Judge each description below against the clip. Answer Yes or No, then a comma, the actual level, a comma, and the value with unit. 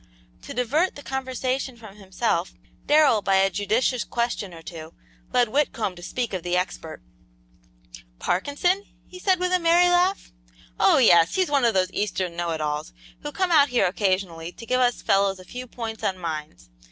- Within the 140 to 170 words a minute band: No, average, 180 wpm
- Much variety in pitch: Yes, wide, 7.4 semitones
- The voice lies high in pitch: Yes, high, 225 Hz